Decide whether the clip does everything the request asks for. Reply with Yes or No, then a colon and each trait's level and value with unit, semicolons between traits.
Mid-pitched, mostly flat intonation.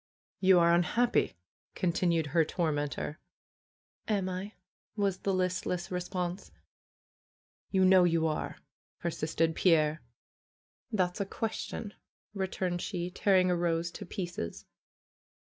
Yes: medium, 180 Hz; narrow, 2.1 semitones